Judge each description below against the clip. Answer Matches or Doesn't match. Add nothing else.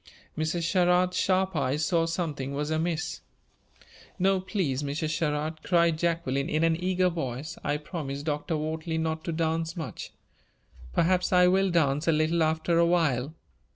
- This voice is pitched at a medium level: Matches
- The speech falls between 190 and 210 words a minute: Doesn't match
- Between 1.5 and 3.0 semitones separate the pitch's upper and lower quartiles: Matches